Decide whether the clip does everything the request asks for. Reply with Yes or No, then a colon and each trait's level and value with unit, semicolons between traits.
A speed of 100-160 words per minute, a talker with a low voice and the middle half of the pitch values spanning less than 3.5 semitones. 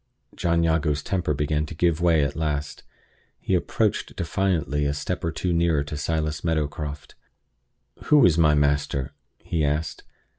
Yes: average, 150 wpm; very low, 75 Hz; narrow, 2.4 semitones